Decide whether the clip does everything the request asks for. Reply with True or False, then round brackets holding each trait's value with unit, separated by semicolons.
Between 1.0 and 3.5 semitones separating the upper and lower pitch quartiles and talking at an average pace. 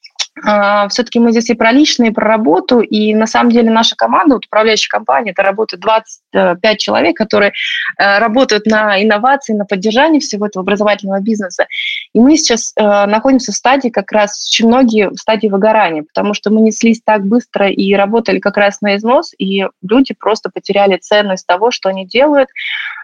False (2.7 semitones; 170 wpm)